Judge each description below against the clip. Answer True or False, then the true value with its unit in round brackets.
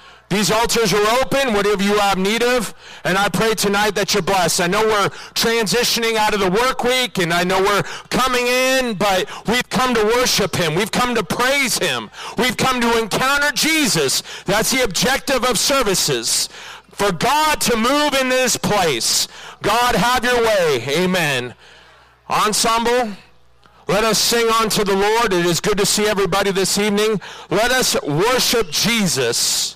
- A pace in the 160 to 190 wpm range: True (165 wpm)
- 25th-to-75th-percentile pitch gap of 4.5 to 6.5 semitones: False (3.7 semitones)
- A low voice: False (220 Hz)